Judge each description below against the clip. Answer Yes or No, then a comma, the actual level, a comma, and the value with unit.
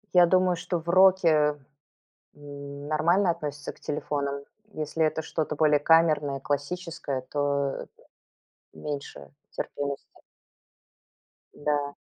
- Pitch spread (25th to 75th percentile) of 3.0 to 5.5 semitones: No, narrow, 2.6 semitones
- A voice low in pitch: No, medium, 150 Hz